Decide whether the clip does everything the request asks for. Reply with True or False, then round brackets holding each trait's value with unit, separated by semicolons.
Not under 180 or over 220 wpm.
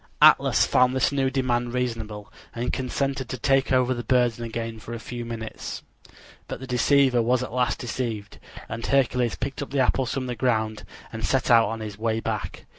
True (190 wpm)